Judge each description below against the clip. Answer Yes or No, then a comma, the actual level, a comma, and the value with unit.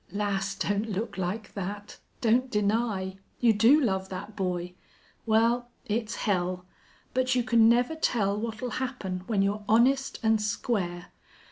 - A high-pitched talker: Yes, high, 210 Hz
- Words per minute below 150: Yes, average, 140 wpm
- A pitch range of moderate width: Yes, average, 3.3 semitones